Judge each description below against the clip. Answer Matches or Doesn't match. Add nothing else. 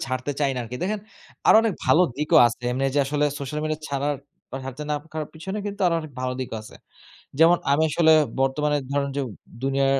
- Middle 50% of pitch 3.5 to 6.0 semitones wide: Doesn't match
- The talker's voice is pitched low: Doesn't match